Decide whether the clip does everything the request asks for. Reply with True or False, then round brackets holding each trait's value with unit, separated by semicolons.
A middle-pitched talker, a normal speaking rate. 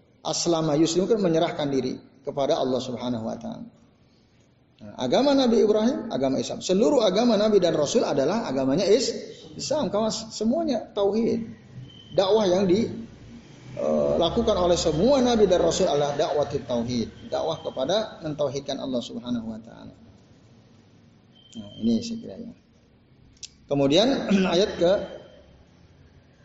True (180 Hz; 115 wpm)